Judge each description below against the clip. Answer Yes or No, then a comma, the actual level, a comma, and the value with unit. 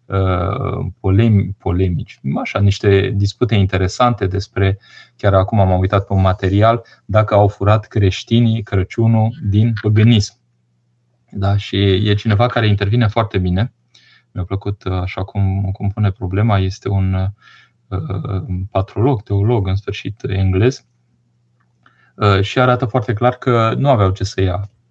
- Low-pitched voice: Yes, low, 100 Hz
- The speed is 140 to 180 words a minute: No, average, 125 wpm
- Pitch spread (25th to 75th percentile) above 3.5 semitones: No, average, 2.9 semitones